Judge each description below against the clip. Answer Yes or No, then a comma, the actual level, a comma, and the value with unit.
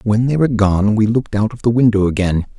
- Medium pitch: No, low, 110 Hz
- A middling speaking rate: No, fast, 255 wpm